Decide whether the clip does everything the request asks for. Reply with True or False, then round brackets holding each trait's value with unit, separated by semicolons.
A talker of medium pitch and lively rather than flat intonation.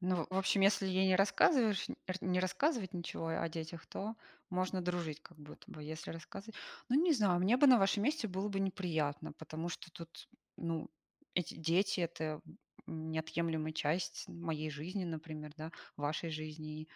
False (170 Hz; 3.4 semitones)